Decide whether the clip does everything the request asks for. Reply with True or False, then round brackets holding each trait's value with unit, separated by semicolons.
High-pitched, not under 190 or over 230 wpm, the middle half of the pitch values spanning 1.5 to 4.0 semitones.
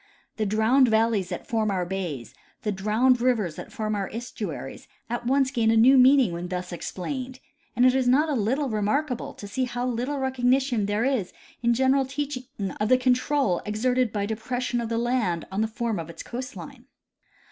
True (235 Hz; 195 wpm; 3.6 semitones)